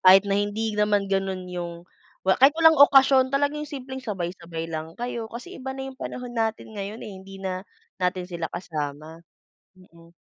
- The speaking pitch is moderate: No, high, 200 Hz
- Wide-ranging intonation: Yes, wide, 6.4 semitones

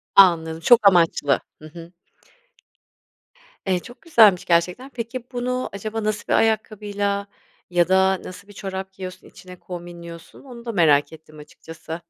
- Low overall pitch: No, high, 190 Hz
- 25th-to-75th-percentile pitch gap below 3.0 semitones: No, average, 4.2 semitones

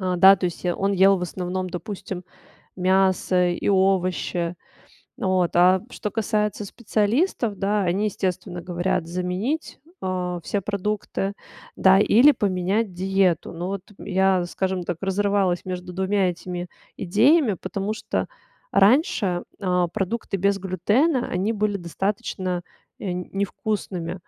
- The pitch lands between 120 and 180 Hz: No, high, 190 Hz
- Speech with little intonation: Yes, narrow, 2.2 semitones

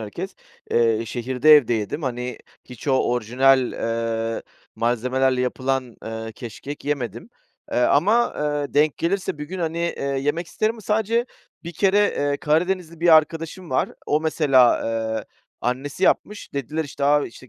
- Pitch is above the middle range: No, medium, 140 Hz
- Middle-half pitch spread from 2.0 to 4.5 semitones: No, average, 5.1 semitones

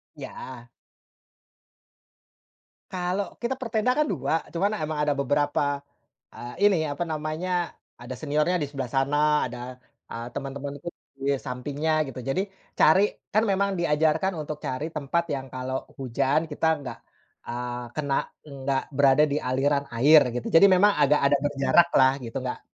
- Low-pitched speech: No, medium, 145 Hz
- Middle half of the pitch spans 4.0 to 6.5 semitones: No, average, 3.3 semitones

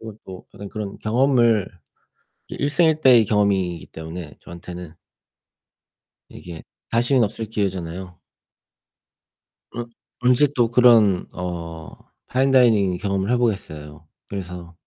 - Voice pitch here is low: Yes, low, 100 Hz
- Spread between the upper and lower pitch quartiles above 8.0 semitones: No, average, 5.1 semitones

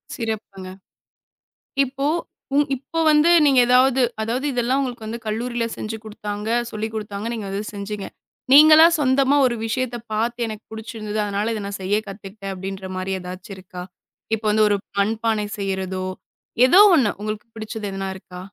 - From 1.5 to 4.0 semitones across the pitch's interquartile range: Yes, average, 3.3 semitones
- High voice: Yes, high, 215 Hz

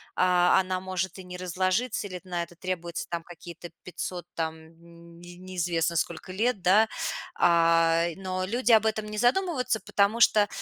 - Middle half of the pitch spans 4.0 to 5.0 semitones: No, average, 3.1 semitones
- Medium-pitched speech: Yes, medium, 180 Hz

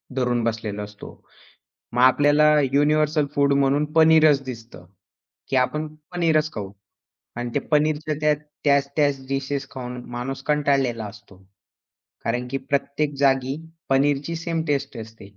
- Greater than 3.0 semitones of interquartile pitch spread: Yes, average, 3.4 semitones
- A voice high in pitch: No, medium, 140 Hz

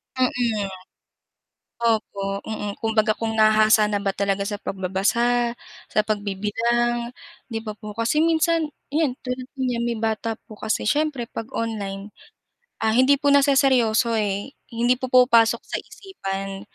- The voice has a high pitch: Yes, high, 225 Hz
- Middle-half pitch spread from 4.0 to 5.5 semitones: No, average, 3.2 semitones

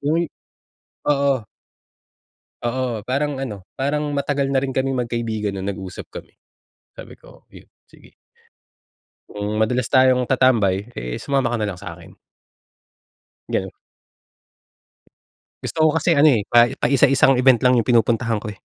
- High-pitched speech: No, low, 125 Hz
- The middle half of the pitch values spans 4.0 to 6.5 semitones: Yes, average, 4.3 semitones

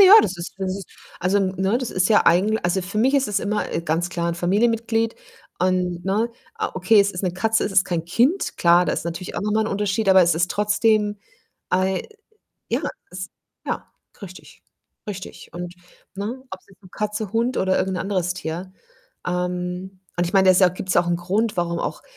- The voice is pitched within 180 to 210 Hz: Yes, high, 190 Hz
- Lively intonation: No, average, 2.7 semitones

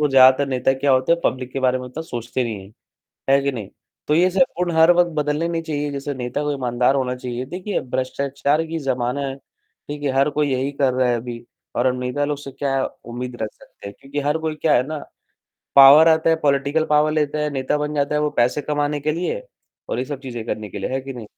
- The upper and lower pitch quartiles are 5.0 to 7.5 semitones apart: No, average, 2.9 semitones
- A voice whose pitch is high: No, medium, 140 Hz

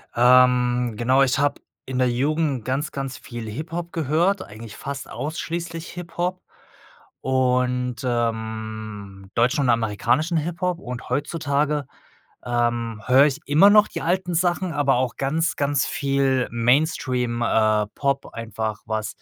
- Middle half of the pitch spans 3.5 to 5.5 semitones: Yes, average, 4.6 semitones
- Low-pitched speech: Yes, low, 130 Hz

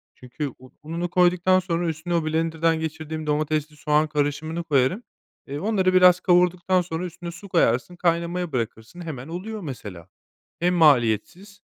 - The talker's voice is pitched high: No, medium, 165 Hz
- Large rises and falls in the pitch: No, average, 3.0 semitones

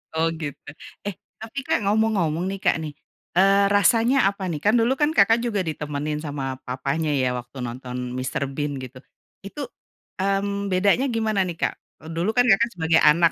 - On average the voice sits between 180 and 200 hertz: Yes, medium, 185 Hz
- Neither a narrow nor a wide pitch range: No, wide, 5.8 semitones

